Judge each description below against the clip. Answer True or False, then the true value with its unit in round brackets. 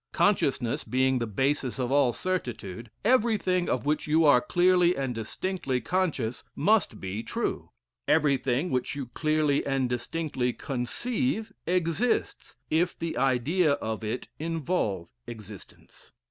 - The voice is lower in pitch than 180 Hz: True (140 Hz)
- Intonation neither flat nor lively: False (6.2 semitones)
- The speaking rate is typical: False (125 wpm)